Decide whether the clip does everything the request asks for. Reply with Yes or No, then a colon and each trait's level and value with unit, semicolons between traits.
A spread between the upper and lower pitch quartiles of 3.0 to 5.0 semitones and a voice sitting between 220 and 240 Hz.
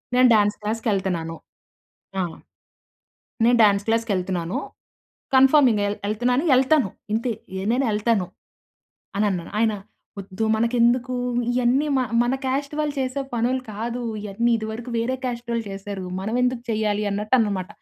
Yes: average, 3.4 semitones; high, 230 Hz